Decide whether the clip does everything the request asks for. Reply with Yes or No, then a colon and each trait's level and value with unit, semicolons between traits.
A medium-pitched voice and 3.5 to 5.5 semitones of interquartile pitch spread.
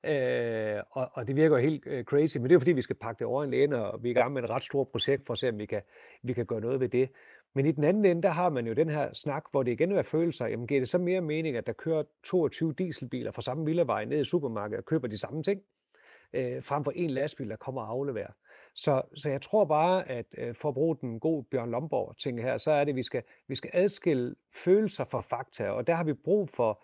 Yes: medium, 145 Hz; average, 4.6 semitones